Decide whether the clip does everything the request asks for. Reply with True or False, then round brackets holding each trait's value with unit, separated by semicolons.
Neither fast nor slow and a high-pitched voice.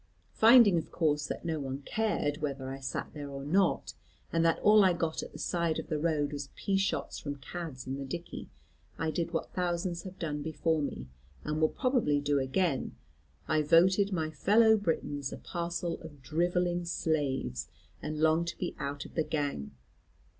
False (185 wpm; 160 Hz)